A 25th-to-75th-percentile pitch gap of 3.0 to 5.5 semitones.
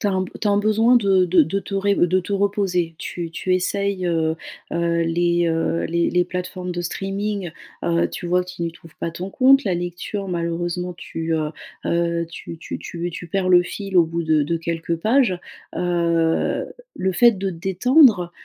No: narrow, 2.5 semitones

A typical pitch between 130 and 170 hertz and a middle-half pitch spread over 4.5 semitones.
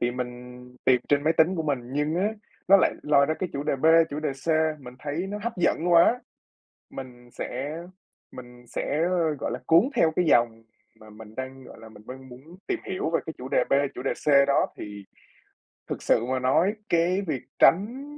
Yes: medium, 140 Hz; average, 5.0 semitones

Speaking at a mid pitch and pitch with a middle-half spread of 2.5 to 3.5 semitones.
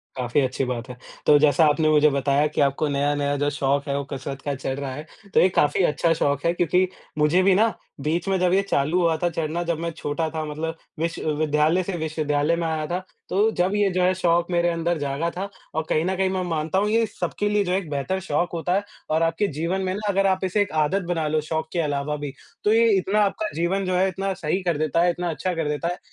No: medium, 165 Hz; average, 3.9 semitones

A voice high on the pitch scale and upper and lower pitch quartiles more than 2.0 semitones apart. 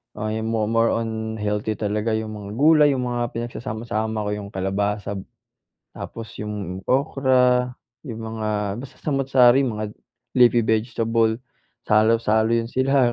No: low, 115 Hz; narrow, 2.5 semitones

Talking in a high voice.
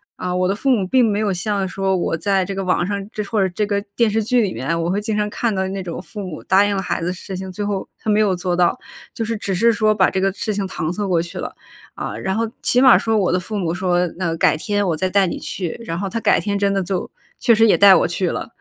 Yes: high, 195 Hz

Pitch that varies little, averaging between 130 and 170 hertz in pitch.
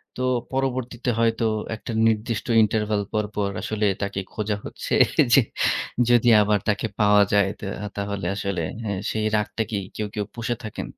No: narrow, 1.9 semitones; low, 105 Hz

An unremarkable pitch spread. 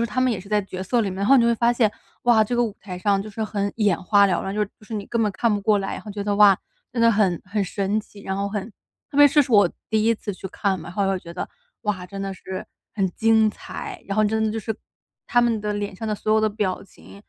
No: narrow, 2.1 semitones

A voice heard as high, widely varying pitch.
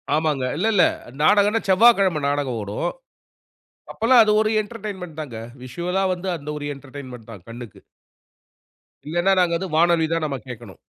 No: medium, 160 Hz; wide, 6.4 semitones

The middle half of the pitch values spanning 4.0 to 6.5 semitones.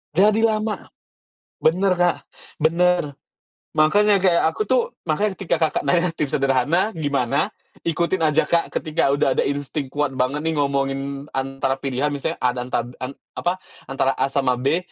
Yes: average, 4.4 semitones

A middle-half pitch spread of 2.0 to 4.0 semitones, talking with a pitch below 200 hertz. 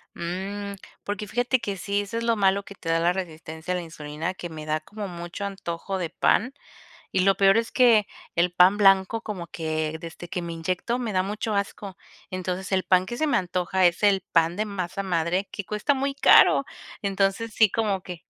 Yes: average, 3.0 semitones; high, 190 Hz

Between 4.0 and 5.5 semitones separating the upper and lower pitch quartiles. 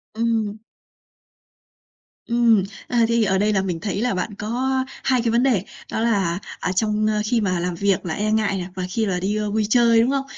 No: average, 3.2 semitones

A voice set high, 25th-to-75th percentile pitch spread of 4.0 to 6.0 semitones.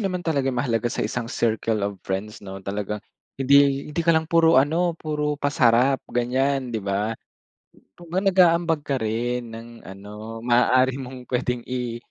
No: low, 125 Hz; average, 4.4 semitones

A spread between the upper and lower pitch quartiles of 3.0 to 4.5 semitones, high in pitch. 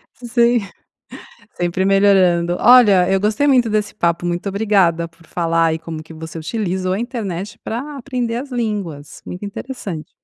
No: average, 5.3 semitones; high, 195 Hz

